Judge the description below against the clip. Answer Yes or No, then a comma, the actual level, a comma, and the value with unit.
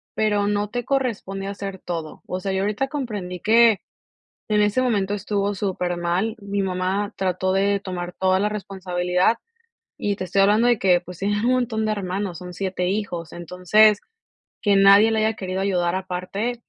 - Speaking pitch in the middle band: No, high, 195 Hz